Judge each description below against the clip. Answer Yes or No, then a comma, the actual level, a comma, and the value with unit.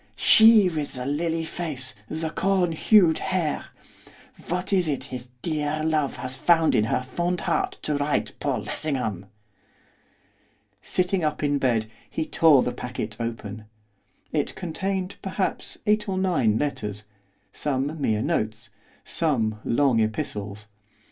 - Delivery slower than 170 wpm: Yes, slow, 135 wpm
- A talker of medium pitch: Yes, medium, 150 Hz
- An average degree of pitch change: No, wide, 6.4 semitones